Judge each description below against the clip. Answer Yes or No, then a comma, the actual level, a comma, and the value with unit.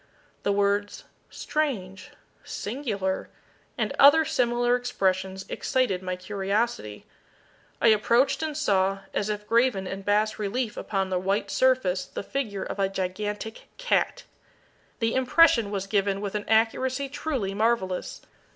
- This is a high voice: Yes, high, 210 Hz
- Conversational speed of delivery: No, slow, 130 wpm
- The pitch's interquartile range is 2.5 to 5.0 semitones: Yes, average, 4.2 semitones